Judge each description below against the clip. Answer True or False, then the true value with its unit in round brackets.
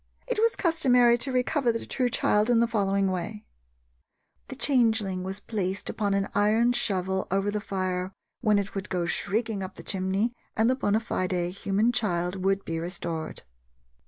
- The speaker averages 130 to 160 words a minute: False (170 wpm)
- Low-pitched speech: False (205 Hz)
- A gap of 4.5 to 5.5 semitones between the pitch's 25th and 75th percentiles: False (3.8 semitones)